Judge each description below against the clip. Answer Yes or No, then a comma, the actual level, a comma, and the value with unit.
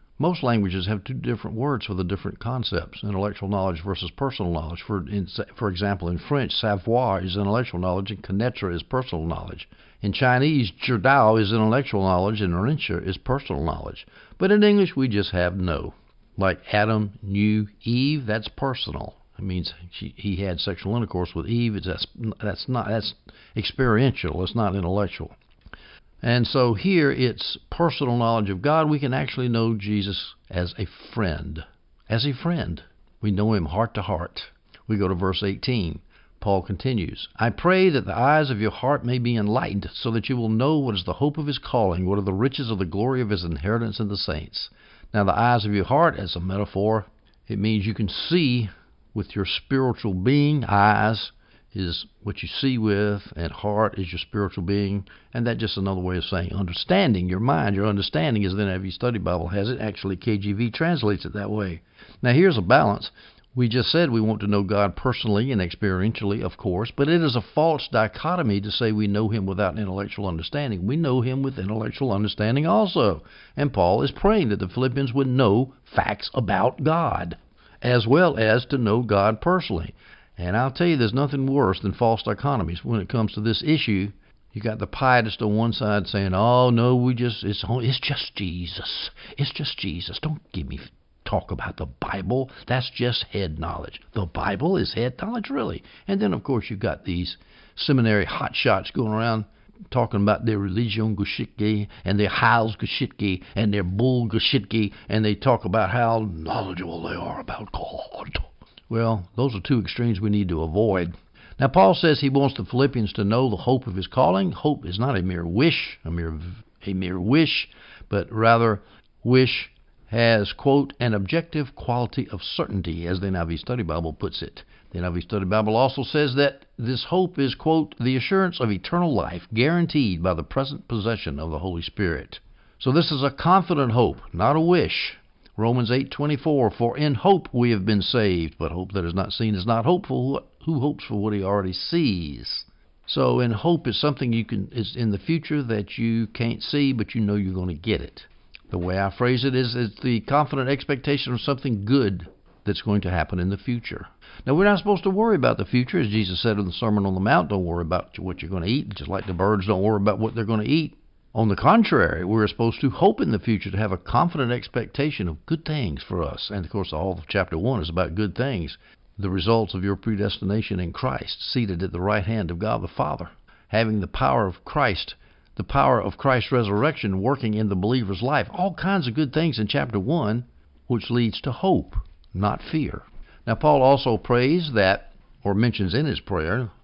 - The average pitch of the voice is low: Yes, low, 110 Hz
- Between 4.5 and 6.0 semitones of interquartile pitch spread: Yes, average, 4.8 semitones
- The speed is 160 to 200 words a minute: Yes, average, 195 wpm